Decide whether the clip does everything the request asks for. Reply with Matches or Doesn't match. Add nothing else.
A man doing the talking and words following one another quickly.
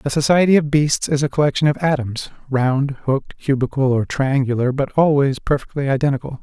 Doesn't match